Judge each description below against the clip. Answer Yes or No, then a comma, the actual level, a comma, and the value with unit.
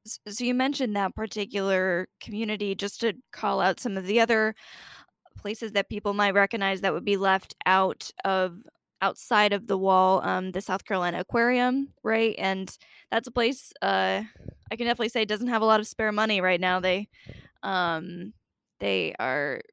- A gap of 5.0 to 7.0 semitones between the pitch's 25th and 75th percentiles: No, average, 2.9 semitones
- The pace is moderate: Yes, average, 175 wpm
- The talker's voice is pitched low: No, high, 205 Hz